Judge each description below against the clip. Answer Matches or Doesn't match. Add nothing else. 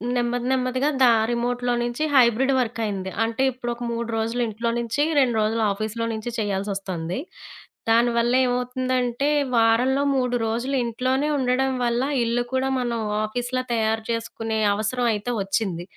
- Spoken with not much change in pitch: Matches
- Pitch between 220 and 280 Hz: Matches